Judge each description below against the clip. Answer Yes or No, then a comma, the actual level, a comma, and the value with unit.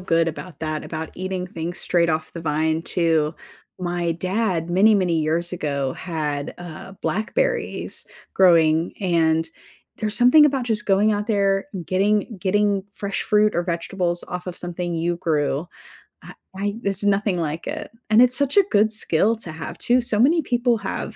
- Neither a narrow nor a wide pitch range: Yes, average, 4.1 semitones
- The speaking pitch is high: No, medium, 180 Hz